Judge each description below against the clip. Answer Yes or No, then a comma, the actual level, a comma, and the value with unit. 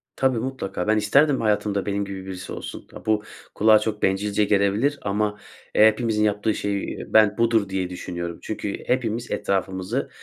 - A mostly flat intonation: Yes, narrow, 2.1 semitones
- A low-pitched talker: Yes, low, 105 Hz